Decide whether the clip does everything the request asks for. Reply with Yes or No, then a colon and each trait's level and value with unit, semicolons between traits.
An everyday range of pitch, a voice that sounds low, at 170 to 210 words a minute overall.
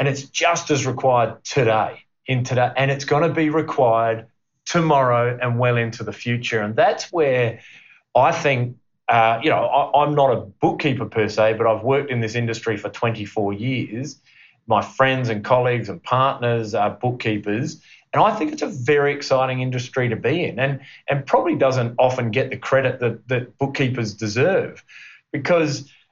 Yes: average, 3.3 semitones; low, 125 Hz; average, 175 wpm